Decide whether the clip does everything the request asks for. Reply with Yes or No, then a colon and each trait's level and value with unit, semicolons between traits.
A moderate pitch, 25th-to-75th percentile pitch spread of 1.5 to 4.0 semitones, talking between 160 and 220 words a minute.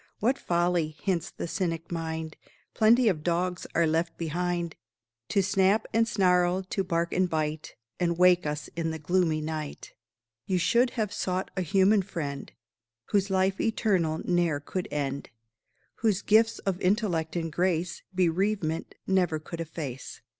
No: medium, 175 Hz; average, 3.0 semitones; average, 145 wpm